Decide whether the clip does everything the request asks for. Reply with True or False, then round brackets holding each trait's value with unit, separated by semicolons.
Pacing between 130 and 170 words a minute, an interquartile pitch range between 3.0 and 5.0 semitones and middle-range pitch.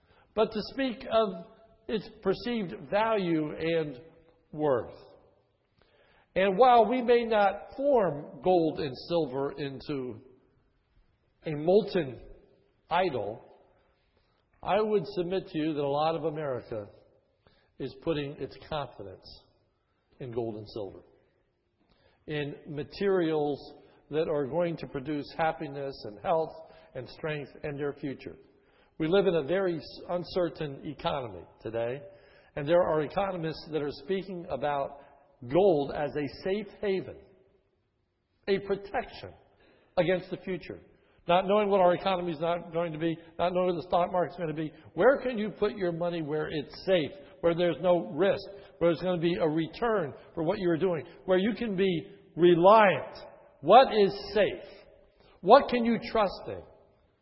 True (145 wpm; 4.6 semitones; 170 Hz)